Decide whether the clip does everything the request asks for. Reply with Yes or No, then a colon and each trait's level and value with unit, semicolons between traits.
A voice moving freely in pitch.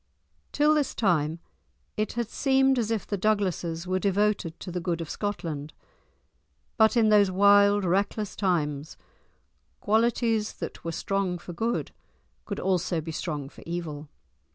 No: average, 4.1 semitones